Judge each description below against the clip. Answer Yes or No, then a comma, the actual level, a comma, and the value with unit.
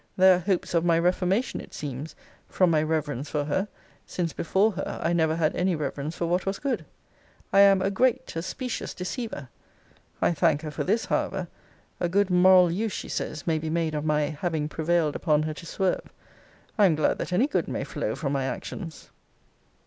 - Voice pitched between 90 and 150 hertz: No, medium, 170 Hz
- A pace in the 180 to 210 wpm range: Yes, average, 200 wpm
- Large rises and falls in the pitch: No, average, 3.5 semitones